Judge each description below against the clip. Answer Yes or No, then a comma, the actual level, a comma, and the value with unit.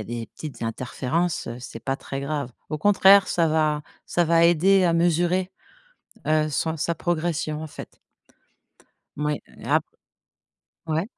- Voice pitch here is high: No, medium, 160 Hz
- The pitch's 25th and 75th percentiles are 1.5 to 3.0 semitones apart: Yes, average, 2.7 semitones